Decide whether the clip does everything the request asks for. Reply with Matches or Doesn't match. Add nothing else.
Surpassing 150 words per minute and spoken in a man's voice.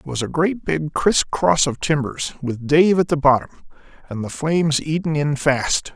Matches